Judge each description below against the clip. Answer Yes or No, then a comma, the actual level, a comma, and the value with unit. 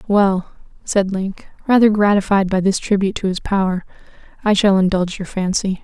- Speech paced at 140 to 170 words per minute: Yes, average, 165 wpm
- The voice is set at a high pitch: Yes, high, 195 Hz